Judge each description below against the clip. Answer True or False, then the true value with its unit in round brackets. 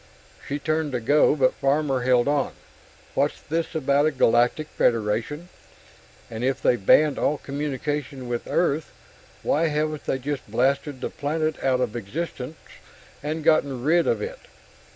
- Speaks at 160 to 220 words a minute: False (150 wpm)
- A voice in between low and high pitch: True (145 Hz)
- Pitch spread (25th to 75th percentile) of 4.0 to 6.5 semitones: False (3.2 semitones)